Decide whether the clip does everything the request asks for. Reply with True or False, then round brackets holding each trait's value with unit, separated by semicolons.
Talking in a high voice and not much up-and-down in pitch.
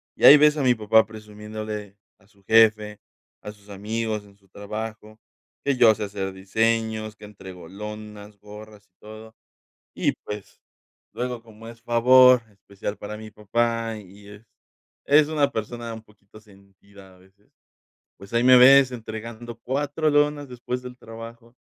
False (110 Hz; 2.3 semitones)